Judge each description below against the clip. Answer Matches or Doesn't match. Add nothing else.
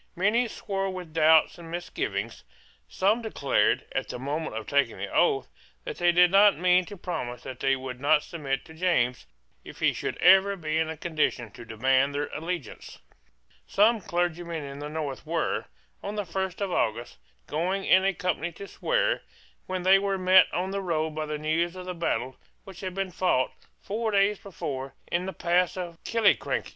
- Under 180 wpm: Doesn't match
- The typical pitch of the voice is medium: Matches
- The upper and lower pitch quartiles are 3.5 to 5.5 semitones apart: Matches